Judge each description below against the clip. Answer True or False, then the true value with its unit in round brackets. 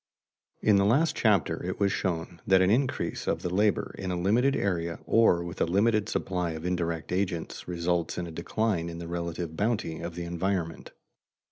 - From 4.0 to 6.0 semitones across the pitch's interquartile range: False (3.0 semitones)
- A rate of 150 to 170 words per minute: False (190 wpm)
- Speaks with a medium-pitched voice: False (90 Hz)